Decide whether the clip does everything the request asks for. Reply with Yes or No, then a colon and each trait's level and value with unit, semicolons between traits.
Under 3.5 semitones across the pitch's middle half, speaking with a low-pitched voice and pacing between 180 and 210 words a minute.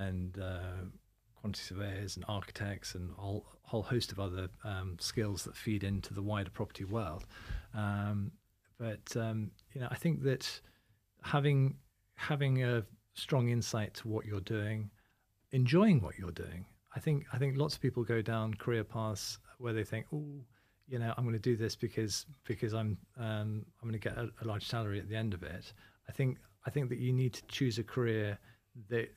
Yes: average, 3.0 semitones; low, 110 Hz; average, 190 wpm